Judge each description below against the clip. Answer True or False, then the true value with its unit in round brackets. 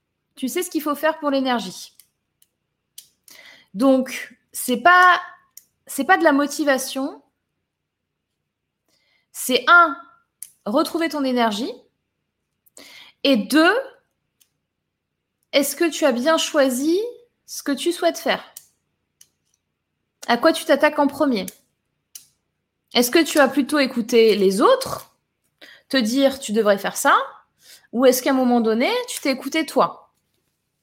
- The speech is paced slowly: True (125 wpm)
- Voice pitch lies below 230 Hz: False (285 Hz)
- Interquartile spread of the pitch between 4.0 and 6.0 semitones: True (4.4 semitones)